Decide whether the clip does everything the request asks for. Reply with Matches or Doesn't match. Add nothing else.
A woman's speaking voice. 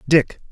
Doesn't match